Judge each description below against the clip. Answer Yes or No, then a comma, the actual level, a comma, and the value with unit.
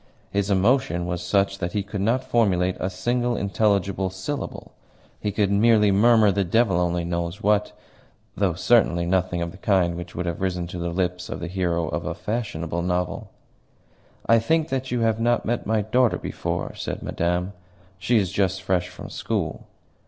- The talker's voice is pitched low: Yes, very low, 95 Hz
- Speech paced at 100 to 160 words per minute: No, average, 180 wpm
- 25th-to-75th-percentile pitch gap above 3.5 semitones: Yes, average, 3.9 semitones